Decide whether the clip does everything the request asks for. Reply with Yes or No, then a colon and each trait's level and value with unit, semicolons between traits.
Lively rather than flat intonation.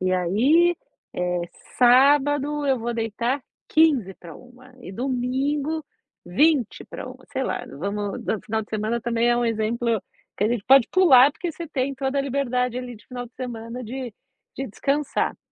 No: average, 3.7 semitones